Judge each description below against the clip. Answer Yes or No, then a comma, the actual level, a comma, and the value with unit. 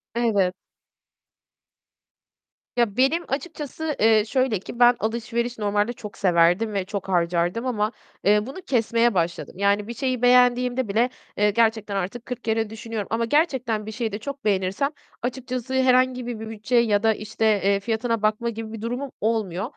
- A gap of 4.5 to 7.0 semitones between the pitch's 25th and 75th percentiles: No, average, 3.0 semitones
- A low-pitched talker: No, high, 225 Hz